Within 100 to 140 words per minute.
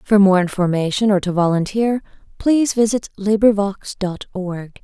Yes: slow, 135 wpm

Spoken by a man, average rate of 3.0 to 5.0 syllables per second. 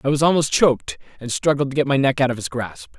No: male; 6.5 syllables/s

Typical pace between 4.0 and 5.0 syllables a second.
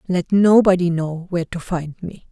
Yes: 4.9 syllables/s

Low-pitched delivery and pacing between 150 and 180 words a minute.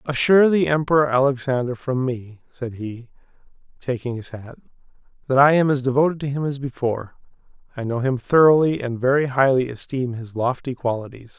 Yes: low, 130 Hz; average, 165 wpm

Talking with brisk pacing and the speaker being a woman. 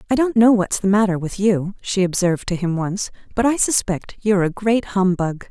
Yes: fast, 220 wpm; female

